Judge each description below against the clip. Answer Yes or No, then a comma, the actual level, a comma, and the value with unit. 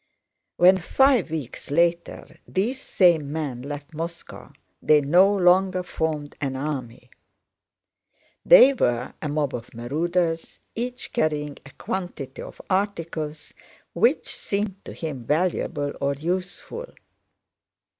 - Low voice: No, medium, 165 Hz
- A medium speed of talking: No, slow, 115 wpm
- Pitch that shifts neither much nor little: Yes, average, 4.4 semitones